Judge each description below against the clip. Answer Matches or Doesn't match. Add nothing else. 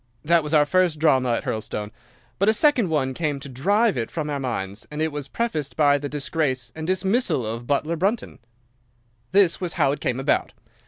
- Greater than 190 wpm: Matches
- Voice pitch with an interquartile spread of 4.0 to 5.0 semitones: Matches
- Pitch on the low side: Doesn't match